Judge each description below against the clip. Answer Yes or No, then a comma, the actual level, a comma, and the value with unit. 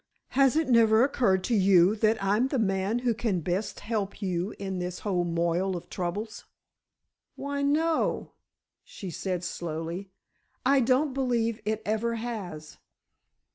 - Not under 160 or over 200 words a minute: No, average, 140 wpm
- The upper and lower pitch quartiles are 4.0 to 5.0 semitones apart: Yes, average, 4.7 semitones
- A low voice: No, high, 210 Hz